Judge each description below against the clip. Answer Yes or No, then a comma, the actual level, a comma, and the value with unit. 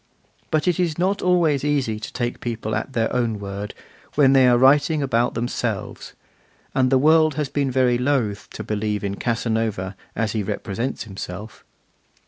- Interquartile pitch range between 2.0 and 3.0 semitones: No, average, 4.7 semitones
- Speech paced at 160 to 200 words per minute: Yes, average, 165 wpm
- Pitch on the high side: No, low, 120 Hz